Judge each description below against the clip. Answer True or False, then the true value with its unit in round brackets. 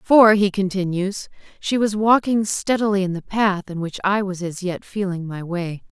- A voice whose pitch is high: True (195 Hz)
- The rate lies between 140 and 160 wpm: False (190 wpm)